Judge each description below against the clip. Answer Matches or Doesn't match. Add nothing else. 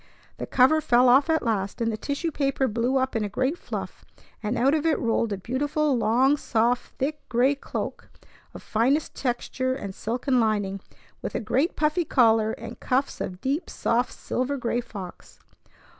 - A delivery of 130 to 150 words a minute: Doesn't match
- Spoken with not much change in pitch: Doesn't match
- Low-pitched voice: Doesn't match